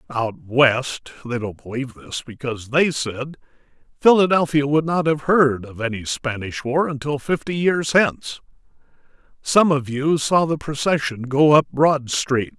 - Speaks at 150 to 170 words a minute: Yes, average, 155 wpm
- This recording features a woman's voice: No, male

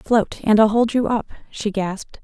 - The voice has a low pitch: No, high, 215 Hz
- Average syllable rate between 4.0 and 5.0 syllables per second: Yes, 4.7 syllables/s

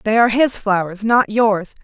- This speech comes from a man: No, female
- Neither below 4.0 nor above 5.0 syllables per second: Yes, 4.9 syllables/s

